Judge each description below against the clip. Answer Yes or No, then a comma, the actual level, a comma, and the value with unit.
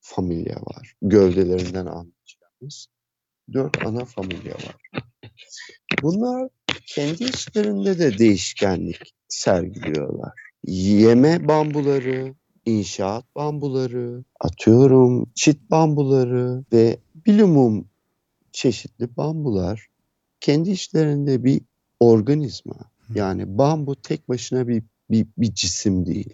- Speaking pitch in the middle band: No, low, 125 Hz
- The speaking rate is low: Yes, slow, 85 wpm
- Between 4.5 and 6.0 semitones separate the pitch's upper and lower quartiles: Yes, average, 5.2 semitones